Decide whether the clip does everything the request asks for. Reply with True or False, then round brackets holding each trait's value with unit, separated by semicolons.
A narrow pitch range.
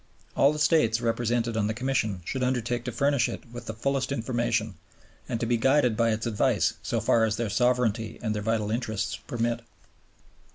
True (2.1 semitones)